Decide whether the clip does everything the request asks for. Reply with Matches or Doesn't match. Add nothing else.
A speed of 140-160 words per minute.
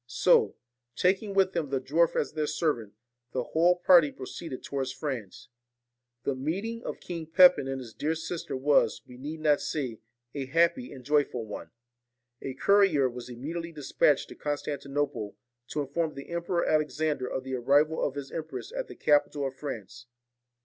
Doesn't match